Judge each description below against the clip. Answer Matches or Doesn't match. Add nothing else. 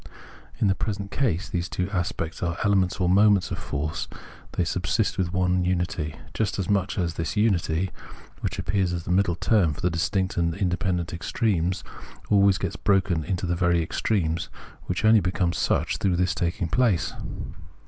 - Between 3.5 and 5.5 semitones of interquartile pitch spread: Doesn't match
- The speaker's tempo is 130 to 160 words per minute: Doesn't match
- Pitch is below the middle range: Matches